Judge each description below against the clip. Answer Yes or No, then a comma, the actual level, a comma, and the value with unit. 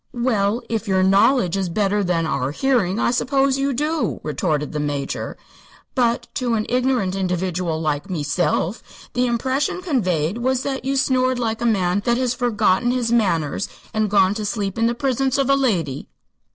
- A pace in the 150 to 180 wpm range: Yes, average, 175 wpm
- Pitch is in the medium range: No, high, 220 Hz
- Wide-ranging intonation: Yes, wide, 5.8 semitones